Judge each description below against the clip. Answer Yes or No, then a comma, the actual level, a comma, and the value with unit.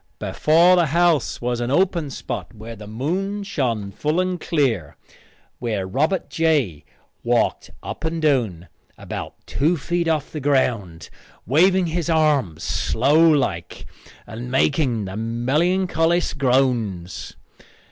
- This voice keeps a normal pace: No, slow, 125 wpm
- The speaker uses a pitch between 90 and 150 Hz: Yes, medium, 140 Hz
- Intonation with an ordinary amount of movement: No, wide, 6.4 semitones